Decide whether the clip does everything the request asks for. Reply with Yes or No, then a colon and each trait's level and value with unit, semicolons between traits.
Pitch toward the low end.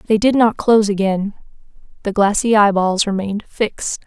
No: high, 205 Hz